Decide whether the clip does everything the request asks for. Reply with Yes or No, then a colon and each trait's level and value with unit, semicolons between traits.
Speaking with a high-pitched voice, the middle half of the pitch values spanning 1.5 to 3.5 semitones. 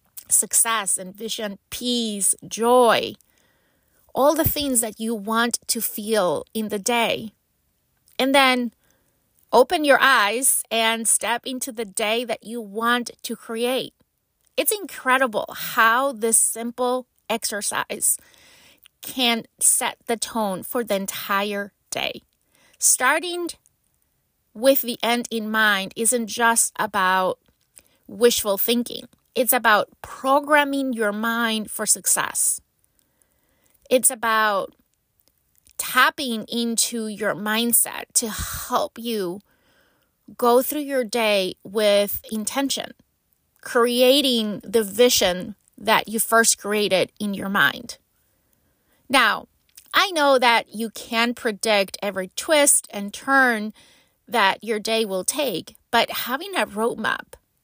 Yes: high, 230 Hz; average, 3.0 semitones